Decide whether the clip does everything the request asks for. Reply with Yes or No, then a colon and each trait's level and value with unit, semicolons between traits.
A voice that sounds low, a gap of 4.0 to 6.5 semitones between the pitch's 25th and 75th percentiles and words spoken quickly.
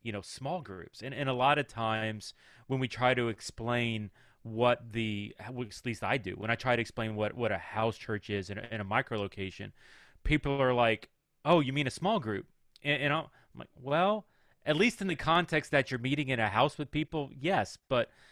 Yes: low, 125 Hz; average, 4.7 semitones; fast, 220 wpm